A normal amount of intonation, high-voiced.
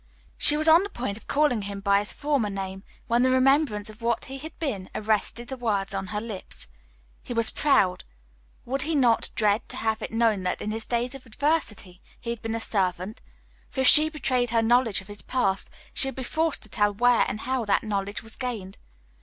Yes: average, 4.1 semitones; high, 230 Hz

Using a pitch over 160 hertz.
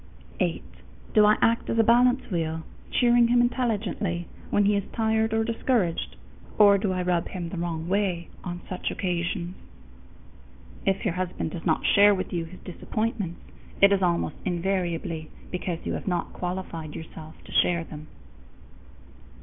Yes: medium, 185 Hz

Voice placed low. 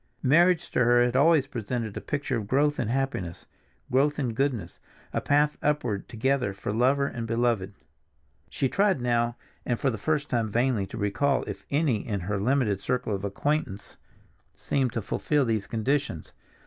Yes: low, 125 Hz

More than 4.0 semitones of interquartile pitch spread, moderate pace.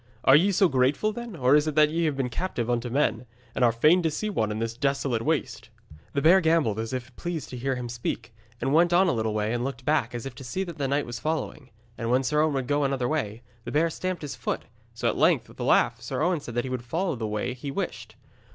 No: average, 4.7 semitones; fast, 270 wpm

